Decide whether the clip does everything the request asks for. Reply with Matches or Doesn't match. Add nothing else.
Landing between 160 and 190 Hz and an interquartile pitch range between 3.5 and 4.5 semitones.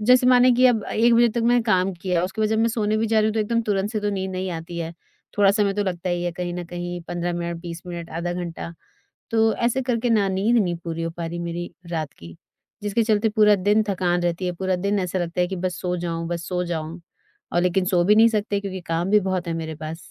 Matches